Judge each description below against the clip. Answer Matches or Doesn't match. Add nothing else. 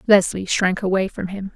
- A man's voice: Doesn't match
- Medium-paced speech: Matches